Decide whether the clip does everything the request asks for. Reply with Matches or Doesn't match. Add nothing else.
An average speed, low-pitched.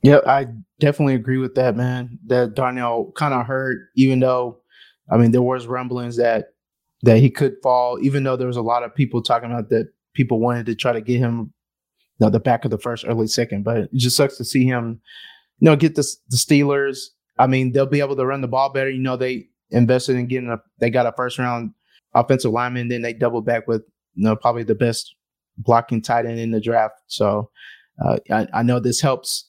Doesn't match